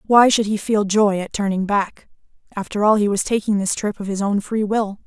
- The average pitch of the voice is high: Yes, high, 205 Hz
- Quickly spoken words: Yes, fast, 235 wpm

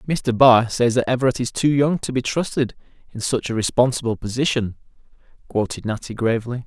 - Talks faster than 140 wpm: Yes, average, 170 wpm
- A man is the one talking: Yes, male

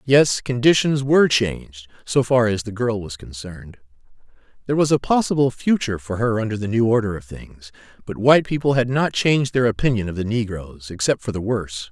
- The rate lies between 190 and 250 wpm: Yes, average, 195 wpm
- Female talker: No, male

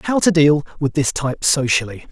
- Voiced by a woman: No, male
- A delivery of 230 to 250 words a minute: No, average, 200 wpm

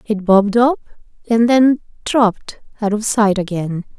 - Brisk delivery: No, average, 150 wpm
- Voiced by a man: No, female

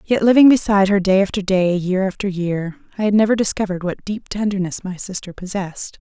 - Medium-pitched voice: No, high, 195 Hz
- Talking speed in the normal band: Yes, average, 195 wpm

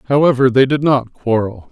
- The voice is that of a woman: No, male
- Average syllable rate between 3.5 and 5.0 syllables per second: Yes, 4.8 syllables/s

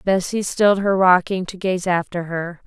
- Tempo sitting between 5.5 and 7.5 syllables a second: No, 4.7 syllables/s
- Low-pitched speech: No, medium, 185 Hz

